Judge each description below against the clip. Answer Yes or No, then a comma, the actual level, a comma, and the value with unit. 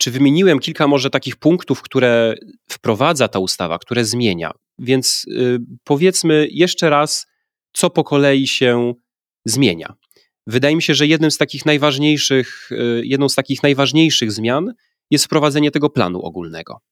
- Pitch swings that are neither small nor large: Yes, average, 3.9 semitones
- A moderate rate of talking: Yes, average, 140 wpm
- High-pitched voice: No, medium, 140 Hz